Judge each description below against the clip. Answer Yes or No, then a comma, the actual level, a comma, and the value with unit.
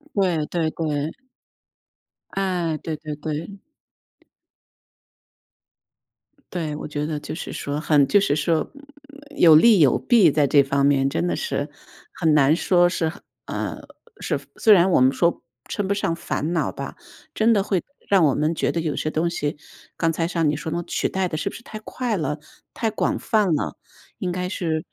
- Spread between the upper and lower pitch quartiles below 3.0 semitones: No, average, 4.0 semitones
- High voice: No, medium, 165 Hz